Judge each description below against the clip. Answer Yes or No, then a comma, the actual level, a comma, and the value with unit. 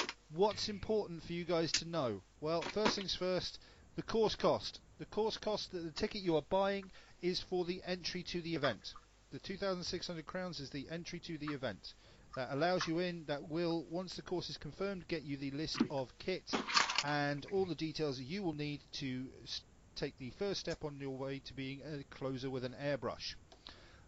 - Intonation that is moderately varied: Yes, average, 4.8 semitones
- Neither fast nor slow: Yes, average, 195 wpm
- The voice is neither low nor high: Yes, medium, 160 Hz